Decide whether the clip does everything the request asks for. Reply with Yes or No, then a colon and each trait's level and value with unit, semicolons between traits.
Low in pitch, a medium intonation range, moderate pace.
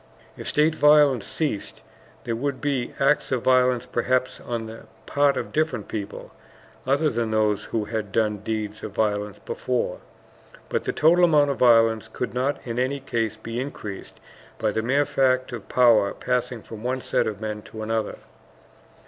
Yes: low, 120 Hz; average, 3.7 semitones; average, 170 wpm